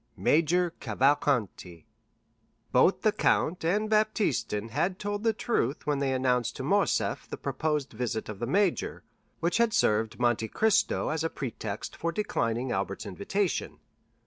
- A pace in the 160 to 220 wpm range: No, average, 145 wpm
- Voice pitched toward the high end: No, medium, 145 Hz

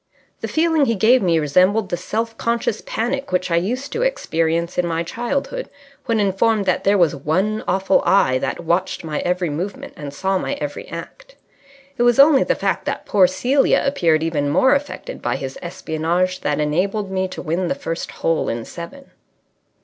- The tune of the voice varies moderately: No, wide, 6.0 semitones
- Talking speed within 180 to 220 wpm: Yes, average, 185 wpm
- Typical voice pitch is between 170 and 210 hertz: Yes, high, 190 Hz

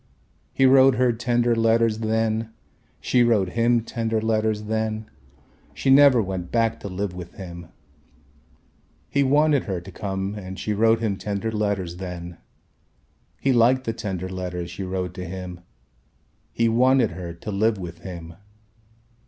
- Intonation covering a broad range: No, average, 3.9 semitones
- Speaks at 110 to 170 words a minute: Yes, average, 150 wpm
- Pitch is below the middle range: Yes, low, 110 Hz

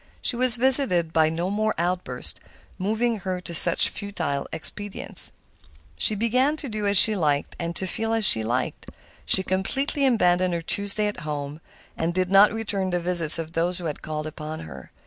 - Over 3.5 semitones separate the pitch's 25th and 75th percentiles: Yes, average, 4.6 semitones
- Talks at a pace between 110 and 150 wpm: No, average, 185 wpm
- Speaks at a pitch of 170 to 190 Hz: Yes, medium, 185 Hz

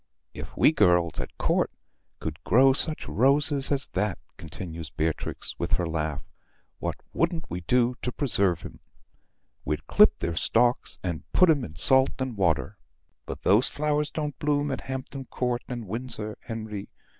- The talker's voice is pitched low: Yes, low, 120 Hz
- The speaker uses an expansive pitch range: Yes, wide, 7.6 semitones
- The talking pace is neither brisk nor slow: Yes, average, 155 wpm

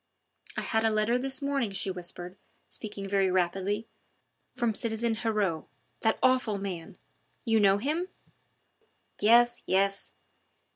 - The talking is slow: Yes, slow, 125 wpm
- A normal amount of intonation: Yes, average, 3.3 semitones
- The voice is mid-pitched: No, high, 215 Hz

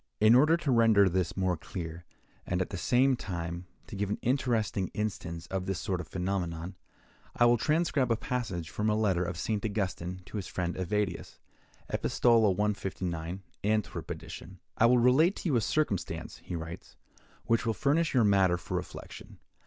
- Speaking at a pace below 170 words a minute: No, average, 175 wpm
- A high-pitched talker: No, low, 100 Hz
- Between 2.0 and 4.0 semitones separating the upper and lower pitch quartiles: No, average, 4.5 semitones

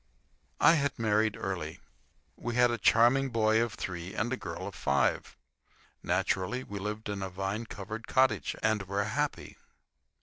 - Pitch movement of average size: Yes, average, 3.4 semitones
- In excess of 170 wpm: No, average, 160 wpm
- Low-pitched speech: Yes, low, 110 Hz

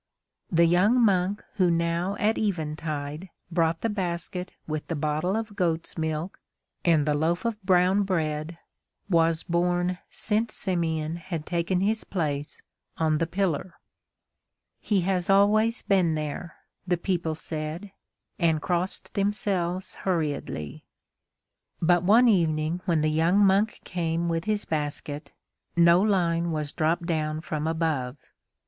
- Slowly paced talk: Yes, slow, 130 wpm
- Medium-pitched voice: Yes, medium, 170 Hz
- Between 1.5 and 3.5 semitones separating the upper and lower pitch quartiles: Yes, average, 3.2 semitones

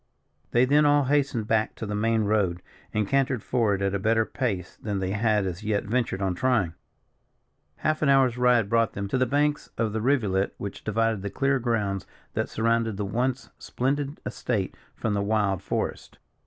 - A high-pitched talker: No, low, 110 Hz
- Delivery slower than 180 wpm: No, average, 185 wpm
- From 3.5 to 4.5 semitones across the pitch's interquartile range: Yes, average, 4.1 semitones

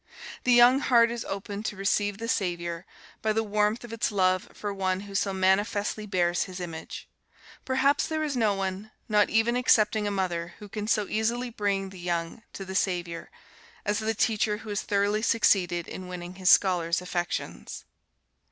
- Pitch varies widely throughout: No, average, 3.0 semitones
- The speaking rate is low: No, average, 180 wpm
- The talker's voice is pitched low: No, high, 205 Hz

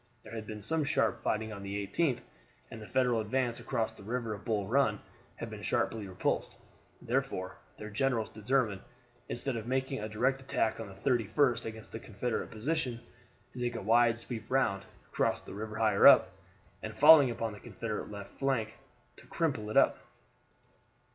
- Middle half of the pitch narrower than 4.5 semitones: Yes, average, 3.2 semitones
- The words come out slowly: No, average, 175 wpm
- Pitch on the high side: No, low, 115 Hz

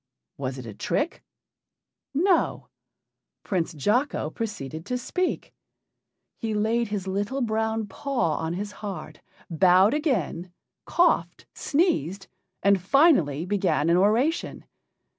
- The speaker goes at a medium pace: No, slow, 110 wpm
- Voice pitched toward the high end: Yes, high, 205 Hz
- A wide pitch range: Yes, wide, 6.5 semitones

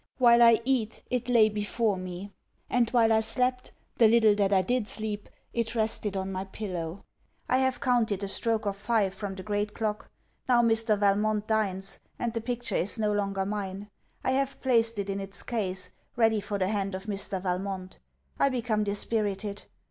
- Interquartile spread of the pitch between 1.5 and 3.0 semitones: Yes, average, 2.7 semitones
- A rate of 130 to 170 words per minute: No, average, 185 wpm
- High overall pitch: Yes, high, 210 Hz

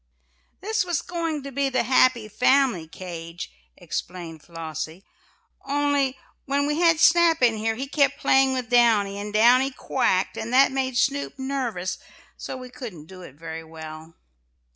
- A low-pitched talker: No, very high, 250 Hz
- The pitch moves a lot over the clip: Yes, wide, 7.1 semitones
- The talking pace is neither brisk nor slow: Yes, average, 155 wpm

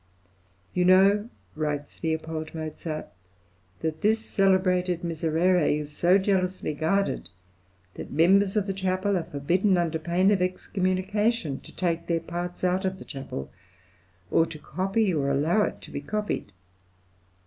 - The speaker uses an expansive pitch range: No, average, 3.3 semitones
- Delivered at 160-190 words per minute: No, average, 140 wpm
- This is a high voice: No, medium, 180 Hz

